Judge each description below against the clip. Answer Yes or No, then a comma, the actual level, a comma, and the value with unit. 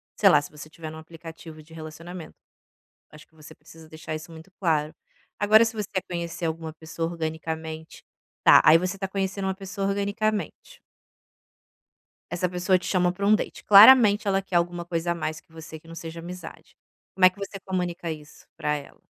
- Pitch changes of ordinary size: Yes, average, 3.2 semitones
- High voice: No, medium, 170 Hz